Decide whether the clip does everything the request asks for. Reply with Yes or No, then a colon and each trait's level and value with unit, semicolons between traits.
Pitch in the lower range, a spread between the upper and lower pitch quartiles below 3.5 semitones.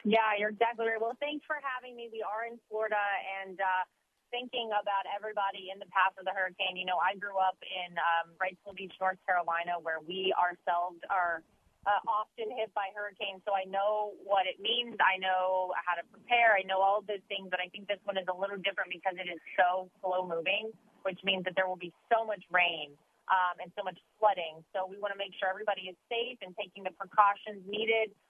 No: high, 195 Hz; narrow, 2.4 semitones